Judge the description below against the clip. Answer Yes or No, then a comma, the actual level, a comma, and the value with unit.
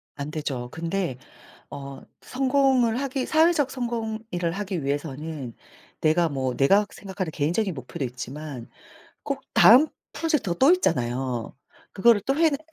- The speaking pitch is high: No, medium, 175 Hz